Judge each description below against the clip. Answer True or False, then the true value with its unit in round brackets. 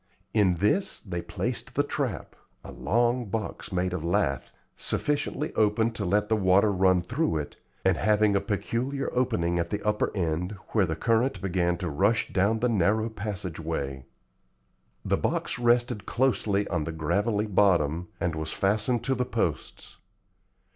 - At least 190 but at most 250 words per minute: False (160 wpm)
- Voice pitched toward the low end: True (100 Hz)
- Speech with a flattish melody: False (4.5 semitones)